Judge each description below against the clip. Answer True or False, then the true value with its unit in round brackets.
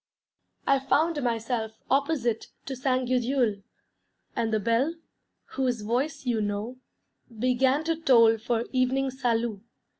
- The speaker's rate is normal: False (120 wpm)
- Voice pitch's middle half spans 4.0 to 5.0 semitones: False (2.9 semitones)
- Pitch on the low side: False (250 Hz)